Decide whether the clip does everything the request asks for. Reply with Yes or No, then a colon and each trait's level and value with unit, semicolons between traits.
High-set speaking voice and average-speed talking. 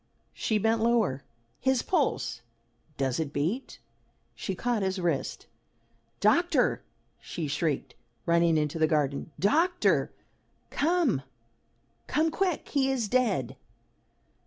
No: high, 205 Hz; slow, 110 wpm